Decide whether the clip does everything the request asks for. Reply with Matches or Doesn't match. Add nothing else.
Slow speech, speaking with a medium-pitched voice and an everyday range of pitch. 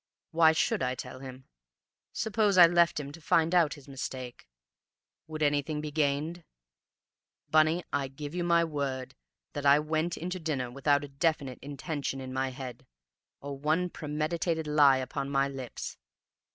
Doesn't match